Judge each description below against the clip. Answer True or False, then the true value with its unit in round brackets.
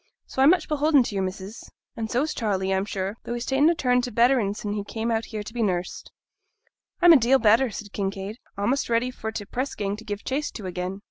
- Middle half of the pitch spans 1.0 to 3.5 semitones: False (4.2 semitones)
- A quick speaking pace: True (240 wpm)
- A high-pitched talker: True (225 Hz)